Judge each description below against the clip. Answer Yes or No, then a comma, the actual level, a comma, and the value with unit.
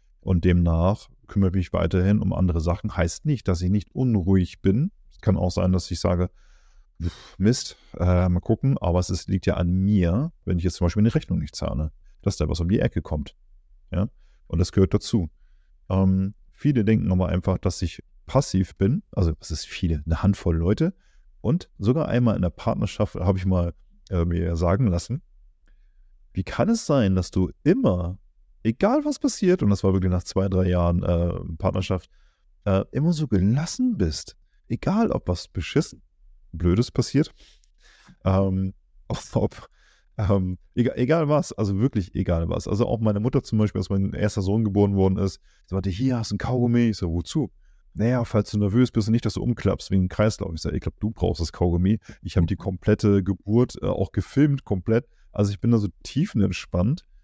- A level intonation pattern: No, average, 3.9 semitones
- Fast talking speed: Yes, fast, 195 wpm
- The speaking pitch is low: Yes, very low, 95 Hz